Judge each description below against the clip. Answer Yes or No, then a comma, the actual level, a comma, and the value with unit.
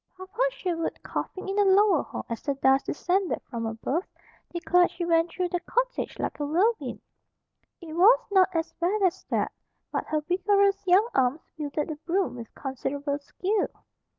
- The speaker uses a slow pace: No, average, 170 wpm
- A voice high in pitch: Yes, very high, 350 Hz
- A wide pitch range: No, average, 4.7 semitones